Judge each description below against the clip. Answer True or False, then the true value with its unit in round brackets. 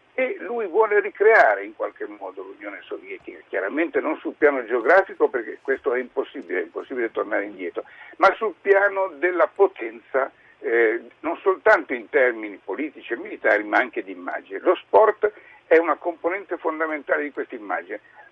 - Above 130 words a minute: True (155 wpm)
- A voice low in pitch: False (380 Hz)